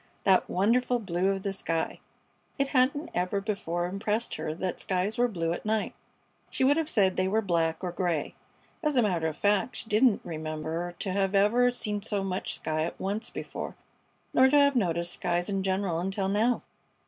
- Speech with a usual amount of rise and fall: Yes, average, 4.2 semitones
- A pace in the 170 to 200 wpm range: Yes, average, 190 wpm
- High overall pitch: Yes, high, 195 Hz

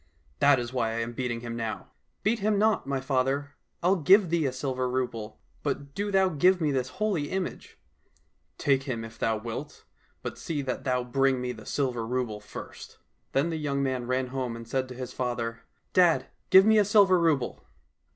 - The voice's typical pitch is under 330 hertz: Yes, low, 135 Hz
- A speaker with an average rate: No, fast, 215 wpm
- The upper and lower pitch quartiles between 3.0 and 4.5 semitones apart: No, average, 5.0 semitones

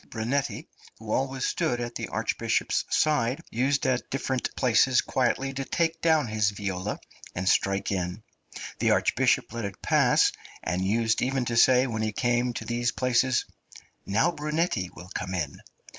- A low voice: Yes, low, 120 Hz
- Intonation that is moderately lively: Yes, average, 4.3 semitones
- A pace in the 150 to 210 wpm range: Yes, average, 160 wpm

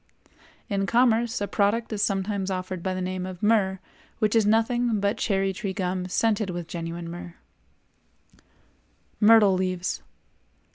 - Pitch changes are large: No, average, 2.9 semitones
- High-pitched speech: Yes, high, 195 Hz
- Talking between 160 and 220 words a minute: No, average, 140 wpm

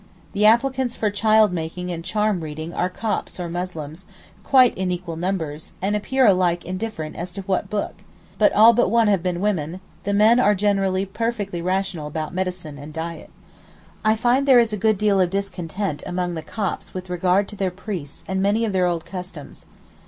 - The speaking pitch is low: No, high, 190 Hz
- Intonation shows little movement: No, average, 3.4 semitones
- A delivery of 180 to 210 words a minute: Yes, average, 190 wpm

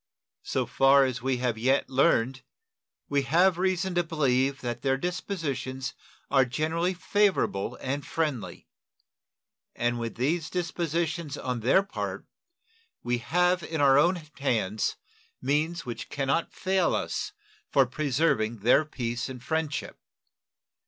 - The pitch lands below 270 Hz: Yes, medium, 140 Hz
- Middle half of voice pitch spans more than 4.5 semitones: Yes, average, 4.9 semitones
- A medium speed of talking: No, slow, 130 wpm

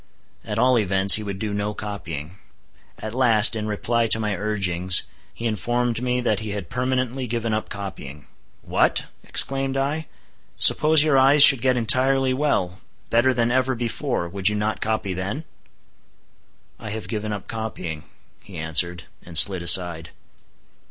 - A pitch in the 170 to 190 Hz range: No, low, 110 Hz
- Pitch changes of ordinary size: Yes, average, 4.5 semitones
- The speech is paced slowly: No, average, 150 wpm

